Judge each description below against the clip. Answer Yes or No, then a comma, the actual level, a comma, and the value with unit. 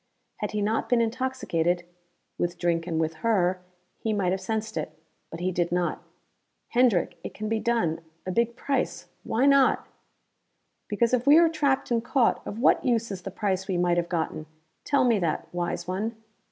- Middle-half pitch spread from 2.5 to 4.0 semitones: No, average, 5.1 semitones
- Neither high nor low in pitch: No, high, 210 Hz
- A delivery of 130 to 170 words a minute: No, average, 185 wpm